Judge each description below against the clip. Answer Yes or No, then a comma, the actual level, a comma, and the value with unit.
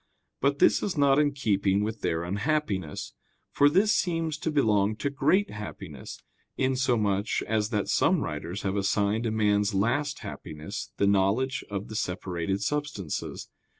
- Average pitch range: No, wide, 6.1 semitones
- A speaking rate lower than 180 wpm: Yes, average, 150 wpm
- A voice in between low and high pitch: No, low, 110 Hz